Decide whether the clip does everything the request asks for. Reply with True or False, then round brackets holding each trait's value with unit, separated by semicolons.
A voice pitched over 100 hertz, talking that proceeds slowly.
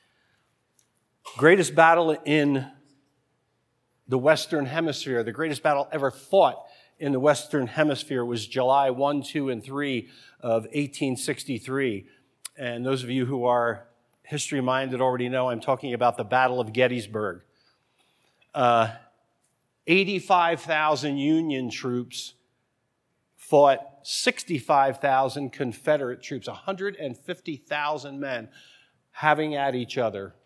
True (135 Hz; 105 wpm)